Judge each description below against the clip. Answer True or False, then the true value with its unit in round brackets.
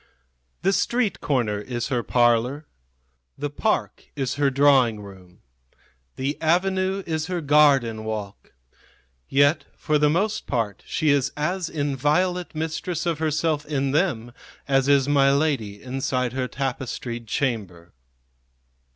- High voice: False (140 Hz)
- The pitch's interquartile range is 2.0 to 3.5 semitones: False (4.4 semitones)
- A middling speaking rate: False (125 wpm)